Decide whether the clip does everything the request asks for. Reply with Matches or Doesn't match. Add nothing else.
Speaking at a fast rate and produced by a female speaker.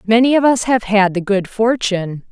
Matches